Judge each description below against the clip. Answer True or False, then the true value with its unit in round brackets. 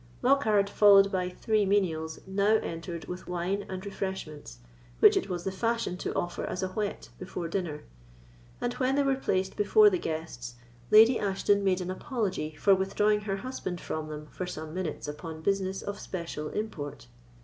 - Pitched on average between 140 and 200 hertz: True (190 Hz)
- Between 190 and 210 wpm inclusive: False (170 wpm)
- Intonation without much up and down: False (3.6 semitones)